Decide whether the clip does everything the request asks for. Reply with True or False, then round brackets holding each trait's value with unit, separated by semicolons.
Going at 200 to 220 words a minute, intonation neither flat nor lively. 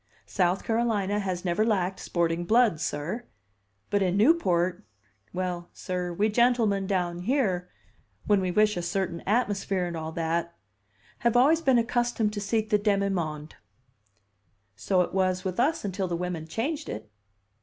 False (155 wpm; 3.8 semitones)